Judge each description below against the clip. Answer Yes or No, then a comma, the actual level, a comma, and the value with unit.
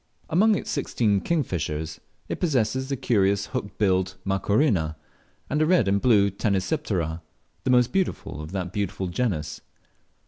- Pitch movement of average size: No, wide, 6.0 semitones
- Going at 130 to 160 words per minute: Yes, average, 140 wpm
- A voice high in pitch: No, low, 100 Hz